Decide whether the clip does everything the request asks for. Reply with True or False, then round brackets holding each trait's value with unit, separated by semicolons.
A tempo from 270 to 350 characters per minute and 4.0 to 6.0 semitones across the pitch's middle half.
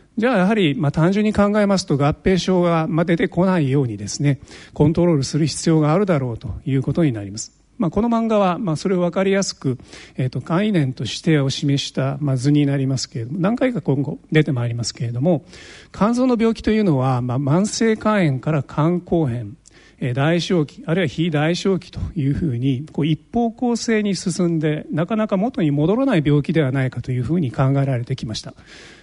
False (405 characters per minute; 5.5 semitones)